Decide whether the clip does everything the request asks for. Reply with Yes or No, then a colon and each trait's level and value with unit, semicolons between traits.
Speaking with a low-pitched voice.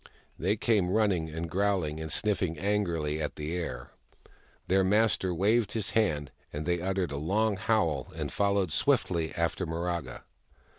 Yes: very low, 90 Hz